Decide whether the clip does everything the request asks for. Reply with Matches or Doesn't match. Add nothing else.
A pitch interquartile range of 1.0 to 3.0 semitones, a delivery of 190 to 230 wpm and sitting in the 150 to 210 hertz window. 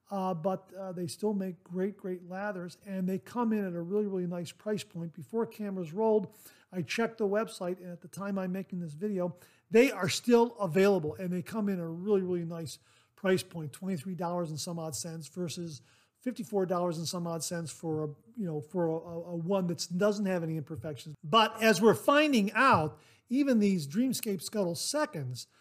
Doesn't match